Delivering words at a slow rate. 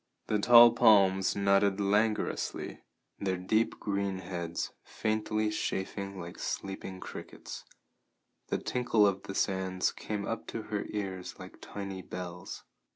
Yes: slow, 125 wpm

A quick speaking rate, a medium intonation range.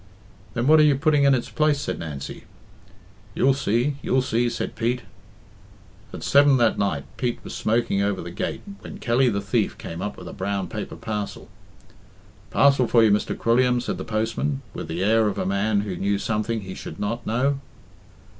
No: average, 190 wpm; average, 4.3 semitones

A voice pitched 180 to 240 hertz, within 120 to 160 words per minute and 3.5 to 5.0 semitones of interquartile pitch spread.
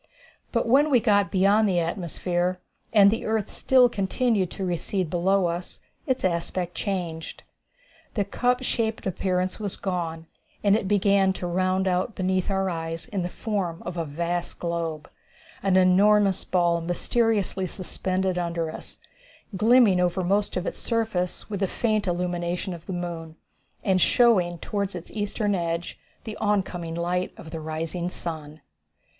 No: medium, 185 Hz; average, 150 wpm; average, 2.9 semitones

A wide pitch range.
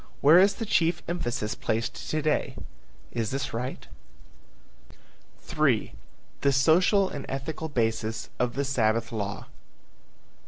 Yes: wide, 5.8 semitones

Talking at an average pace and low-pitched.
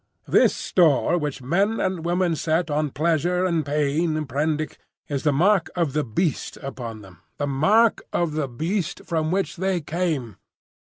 No: average, 155 wpm; medium, 155 Hz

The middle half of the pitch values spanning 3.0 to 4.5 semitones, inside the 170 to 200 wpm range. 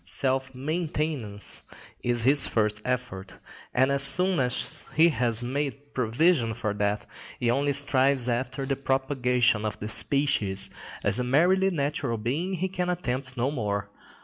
No: average, 3.5 semitones; average, 150 wpm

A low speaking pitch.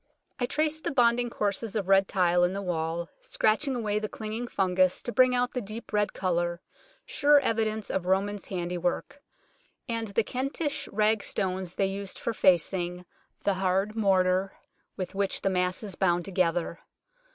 No: high, 195 Hz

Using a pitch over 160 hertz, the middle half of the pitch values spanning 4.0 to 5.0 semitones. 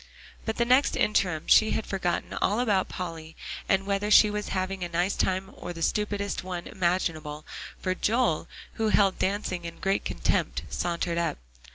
No: high, 190 Hz; average, 3.2 semitones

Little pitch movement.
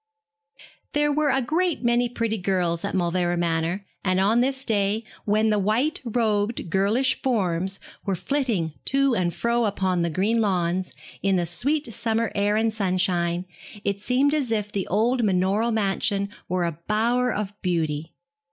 No: average, 4.5 semitones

